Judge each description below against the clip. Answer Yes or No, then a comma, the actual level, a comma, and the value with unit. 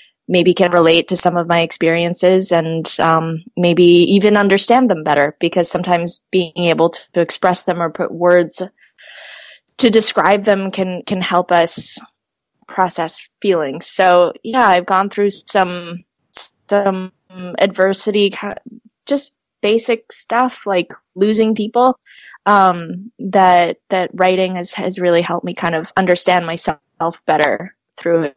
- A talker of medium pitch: Yes, medium, 180 Hz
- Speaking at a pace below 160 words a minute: Yes, slow, 135 wpm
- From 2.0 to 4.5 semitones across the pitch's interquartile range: Yes, average, 2.8 semitones